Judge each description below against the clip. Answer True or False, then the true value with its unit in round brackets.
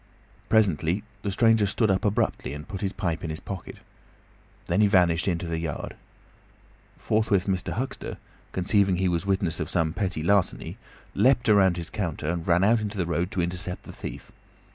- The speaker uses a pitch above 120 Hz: False (95 Hz)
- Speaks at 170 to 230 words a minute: True (180 wpm)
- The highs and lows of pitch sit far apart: False (3.3 semitones)